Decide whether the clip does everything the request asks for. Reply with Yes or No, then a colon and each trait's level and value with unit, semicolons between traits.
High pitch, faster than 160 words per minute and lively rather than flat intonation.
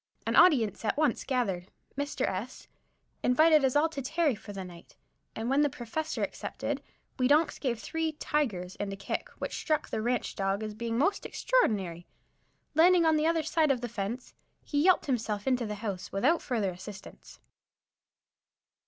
Yes: very high, 250 Hz; average, 170 wpm; wide, 6.8 semitones